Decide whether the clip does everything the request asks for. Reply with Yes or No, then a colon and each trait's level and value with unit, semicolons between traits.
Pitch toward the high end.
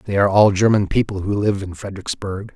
No: low, 100 Hz